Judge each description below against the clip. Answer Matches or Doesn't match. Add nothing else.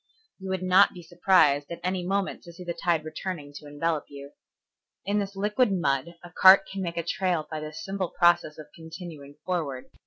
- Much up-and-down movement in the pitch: Doesn't match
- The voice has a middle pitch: Matches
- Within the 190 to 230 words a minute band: Matches